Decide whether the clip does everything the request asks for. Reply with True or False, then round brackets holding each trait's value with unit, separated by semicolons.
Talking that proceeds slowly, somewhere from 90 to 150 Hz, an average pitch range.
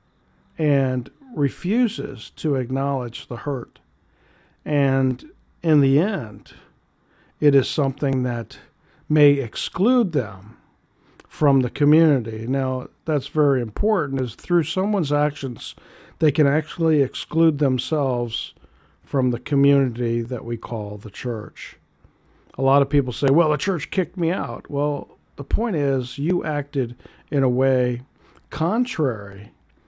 True (125 wpm; 140 Hz; 3.5 semitones)